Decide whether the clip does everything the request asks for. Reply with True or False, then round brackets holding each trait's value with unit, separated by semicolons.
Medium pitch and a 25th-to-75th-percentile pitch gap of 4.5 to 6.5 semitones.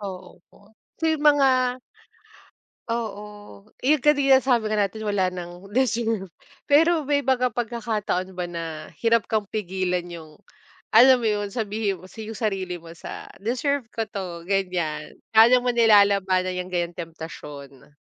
False (205 Hz; 4.8 semitones)